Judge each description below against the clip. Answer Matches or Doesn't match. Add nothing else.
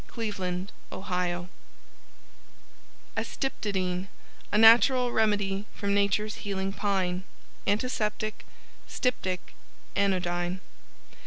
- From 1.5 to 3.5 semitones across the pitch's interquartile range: Matches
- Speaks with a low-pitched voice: Doesn't match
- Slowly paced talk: Matches